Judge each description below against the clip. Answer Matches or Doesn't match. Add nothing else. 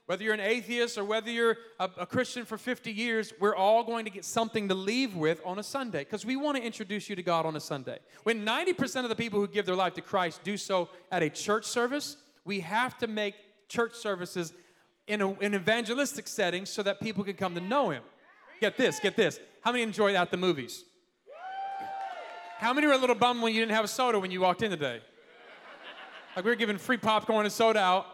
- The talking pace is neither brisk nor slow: Doesn't match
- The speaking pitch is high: Matches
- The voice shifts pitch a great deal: Doesn't match